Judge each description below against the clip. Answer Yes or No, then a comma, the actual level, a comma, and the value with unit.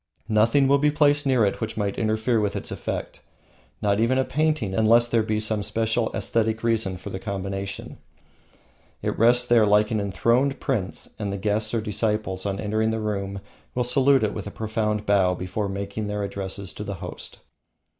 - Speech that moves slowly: No, average, 190 wpm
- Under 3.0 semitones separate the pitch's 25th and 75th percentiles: Yes, narrow, 2.6 semitones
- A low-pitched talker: Yes, low, 110 Hz